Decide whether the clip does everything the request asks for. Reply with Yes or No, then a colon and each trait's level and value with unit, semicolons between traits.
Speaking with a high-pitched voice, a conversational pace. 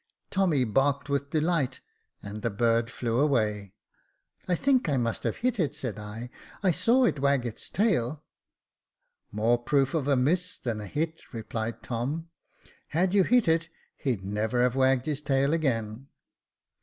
No: low, 135 Hz; average, 170 wpm